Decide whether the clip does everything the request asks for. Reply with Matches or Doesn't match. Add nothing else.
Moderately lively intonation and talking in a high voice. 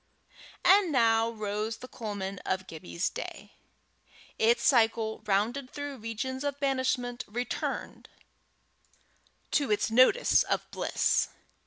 Matches